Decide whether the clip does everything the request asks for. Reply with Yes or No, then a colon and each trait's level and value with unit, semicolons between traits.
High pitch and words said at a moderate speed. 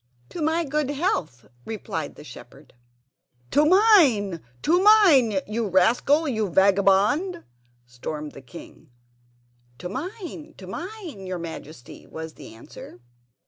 No: high, 220 Hz; slow, 115 wpm